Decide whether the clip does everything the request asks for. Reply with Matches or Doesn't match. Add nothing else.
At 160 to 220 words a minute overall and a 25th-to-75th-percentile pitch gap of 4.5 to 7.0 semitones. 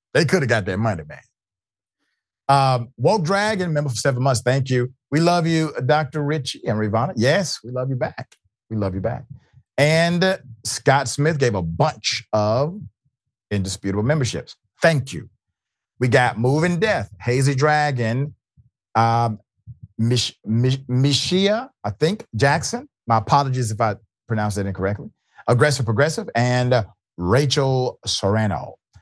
Doesn't match